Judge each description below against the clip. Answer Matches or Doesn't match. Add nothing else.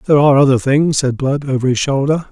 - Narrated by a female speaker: Doesn't match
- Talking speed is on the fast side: Matches